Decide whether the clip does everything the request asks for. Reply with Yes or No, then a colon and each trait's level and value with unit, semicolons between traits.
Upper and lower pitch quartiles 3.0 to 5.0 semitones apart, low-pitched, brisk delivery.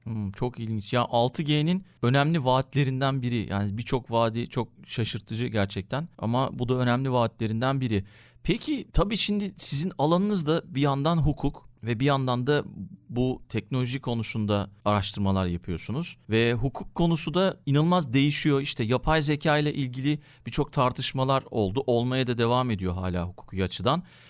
Yes: average, 4.3 semitones; low, 130 Hz; fast, 145 wpm